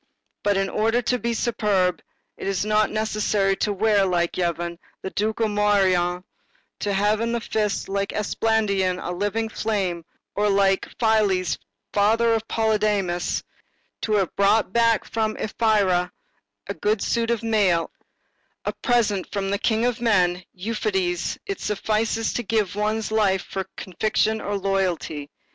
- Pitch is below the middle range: No, high, 205 Hz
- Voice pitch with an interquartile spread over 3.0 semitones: No, narrow, 2.5 semitones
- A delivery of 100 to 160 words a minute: Yes, average, 150 wpm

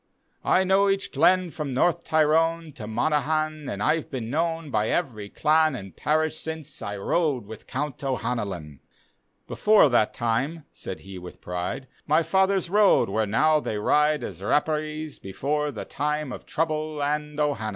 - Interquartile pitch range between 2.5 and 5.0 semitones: No, wide, 5.5 semitones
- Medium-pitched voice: Yes, medium, 150 Hz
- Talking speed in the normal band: Yes, average, 165 wpm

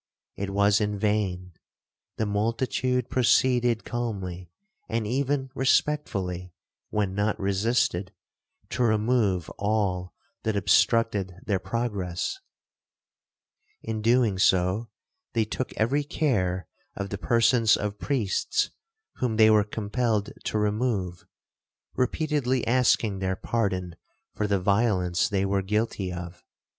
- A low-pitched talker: Yes, low, 105 Hz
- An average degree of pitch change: Yes, average, 3.6 semitones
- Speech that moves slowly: Yes, slow, 110 wpm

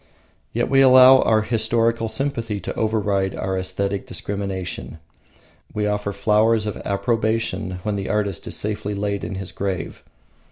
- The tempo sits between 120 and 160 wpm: Yes, average, 145 wpm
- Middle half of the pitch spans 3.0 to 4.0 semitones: No, narrow, 2.4 semitones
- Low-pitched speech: Yes, low, 105 Hz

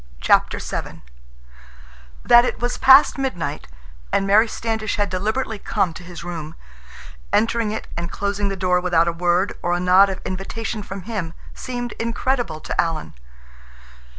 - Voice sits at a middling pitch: No, high, 195 Hz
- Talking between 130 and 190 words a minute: Yes, average, 150 wpm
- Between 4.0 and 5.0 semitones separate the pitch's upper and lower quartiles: Yes, average, 4.4 semitones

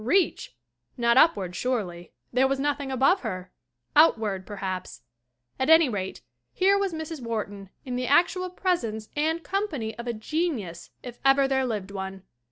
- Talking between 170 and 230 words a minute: No, average, 160 wpm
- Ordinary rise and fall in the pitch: No, wide, 7.5 semitones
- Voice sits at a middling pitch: No, very high, 250 Hz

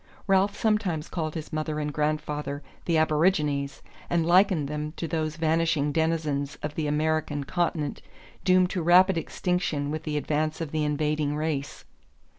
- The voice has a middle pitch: Yes, medium, 155 Hz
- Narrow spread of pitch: Yes, narrow, 2.0 semitones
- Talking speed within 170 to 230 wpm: No, average, 150 wpm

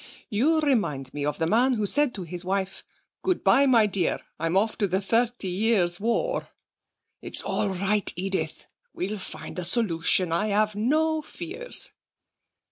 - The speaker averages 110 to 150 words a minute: No, average, 160 wpm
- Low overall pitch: No, high, 205 Hz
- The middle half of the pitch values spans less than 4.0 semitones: No, average, 5.1 semitones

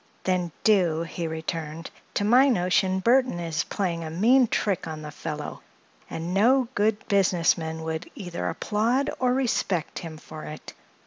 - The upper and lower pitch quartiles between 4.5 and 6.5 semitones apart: Yes, average, 5.2 semitones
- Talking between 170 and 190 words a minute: No, average, 155 wpm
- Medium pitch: Yes, medium, 180 Hz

